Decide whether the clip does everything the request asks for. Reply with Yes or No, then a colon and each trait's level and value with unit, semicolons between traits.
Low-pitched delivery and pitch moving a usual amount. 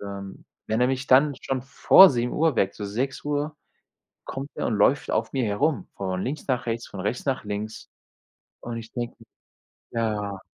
Yes: low, 120 Hz; average, 4.6 semitones